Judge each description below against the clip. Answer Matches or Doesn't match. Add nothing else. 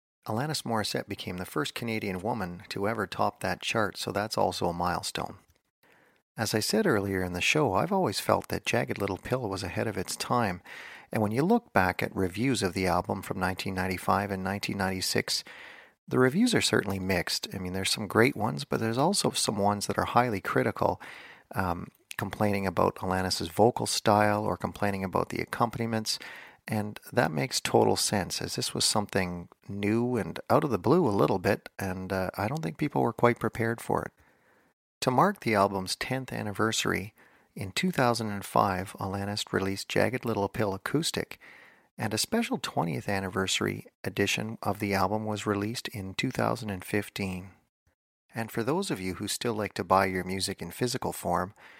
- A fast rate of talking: Doesn't match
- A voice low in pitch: Matches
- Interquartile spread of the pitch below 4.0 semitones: Matches